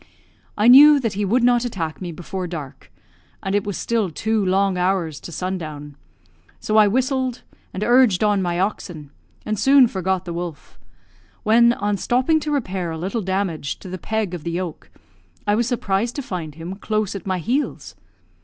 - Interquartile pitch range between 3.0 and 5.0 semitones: Yes, average, 4.7 semitones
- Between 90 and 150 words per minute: No, average, 180 wpm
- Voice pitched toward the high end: Yes, high, 195 Hz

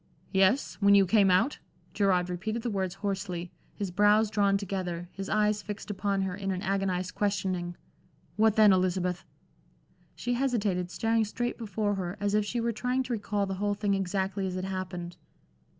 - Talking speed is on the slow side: No, average, 175 wpm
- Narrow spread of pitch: Yes, narrow, 2.2 semitones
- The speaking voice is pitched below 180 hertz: No, high, 200 Hz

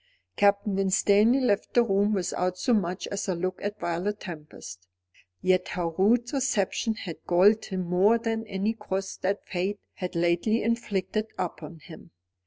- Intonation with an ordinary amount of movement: Yes, average, 3.1 semitones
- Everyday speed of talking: Yes, average, 155 wpm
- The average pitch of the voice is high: Yes, high, 195 Hz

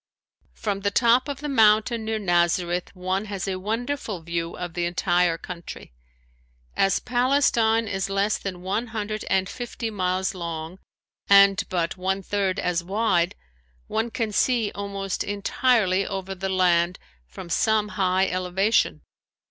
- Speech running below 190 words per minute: Yes, average, 140 wpm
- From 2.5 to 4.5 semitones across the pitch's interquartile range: Yes, average, 3.3 semitones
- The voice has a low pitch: No, high, 195 Hz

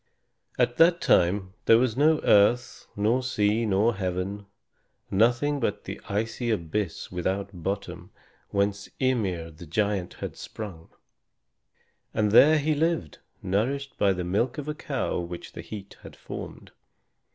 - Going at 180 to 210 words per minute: No, average, 140 wpm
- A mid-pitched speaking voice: No, low, 105 Hz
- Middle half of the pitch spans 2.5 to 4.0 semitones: No, average, 4.5 semitones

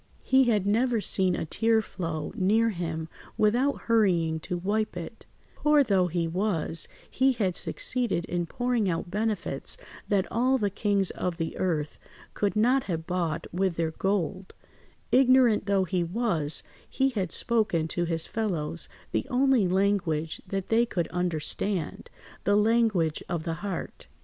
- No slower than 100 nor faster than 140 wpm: No, average, 150 wpm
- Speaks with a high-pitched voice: Yes, high, 195 Hz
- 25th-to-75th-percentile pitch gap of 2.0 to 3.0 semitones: No, average, 4.8 semitones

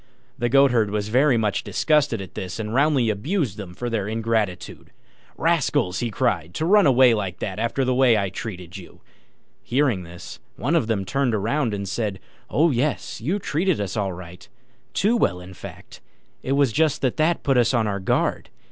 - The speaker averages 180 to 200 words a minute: Yes, average, 190 wpm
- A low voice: Yes, low, 115 Hz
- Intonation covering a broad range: Yes, wide, 5.7 semitones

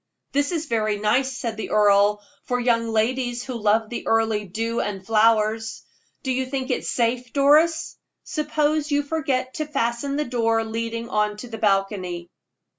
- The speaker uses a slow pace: No, average, 170 wpm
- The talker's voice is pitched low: No, high, 230 Hz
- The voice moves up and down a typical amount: Yes, average, 3.5 semitones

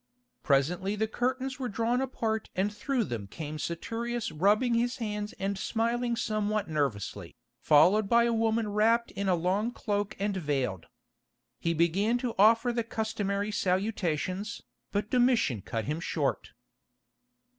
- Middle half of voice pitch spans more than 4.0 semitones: Yes, average, 4.6 semitones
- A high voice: Yes, high, 210 Hz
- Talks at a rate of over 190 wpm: No, average, 140 wpm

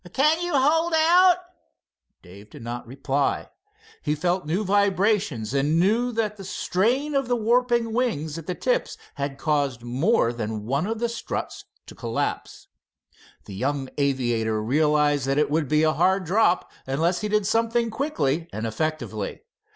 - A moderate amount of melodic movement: No, wide, 8.8 semitones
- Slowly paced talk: No, average, 160 wpm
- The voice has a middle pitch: Yes, medium, 165 Hz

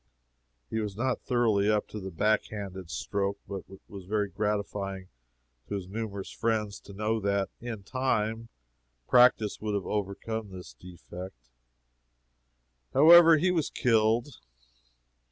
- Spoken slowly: Yes, slow, 130 wpm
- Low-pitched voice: Yes, low, 105 Hz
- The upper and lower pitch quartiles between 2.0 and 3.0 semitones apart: Yes, narrow, 2.6 semitones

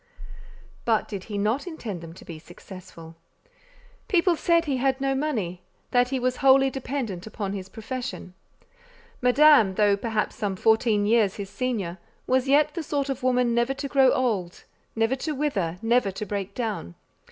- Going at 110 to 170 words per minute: Yes, average, 160 wpm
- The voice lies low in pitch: No, high, 235 Hz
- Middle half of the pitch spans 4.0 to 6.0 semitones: Yes, average, 5.2 semitones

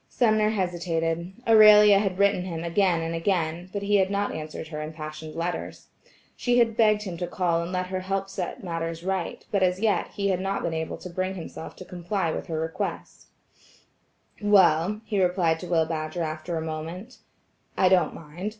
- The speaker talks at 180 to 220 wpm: Yes, average, 185 wpm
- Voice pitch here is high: No, medium, 180 Hz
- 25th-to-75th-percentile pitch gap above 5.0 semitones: No, average, 3.2 semitones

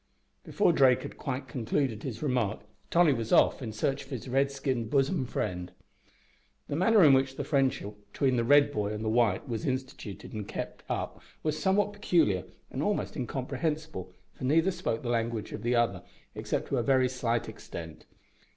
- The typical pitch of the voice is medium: No, low, 130 Hz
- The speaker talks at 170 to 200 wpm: Yes, average, 180 wpm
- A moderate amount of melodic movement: Yes, average, 4.0 semitones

